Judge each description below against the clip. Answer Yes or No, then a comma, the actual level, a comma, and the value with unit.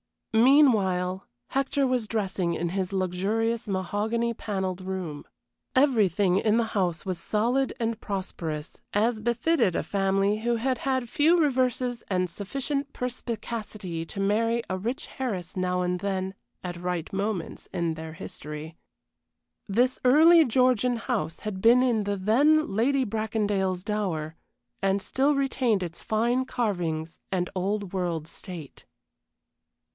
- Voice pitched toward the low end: No, high, 205 Hz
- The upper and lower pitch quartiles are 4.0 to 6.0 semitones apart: Yes, average, 4.8 semitones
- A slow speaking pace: Yes, slow, 130 wpm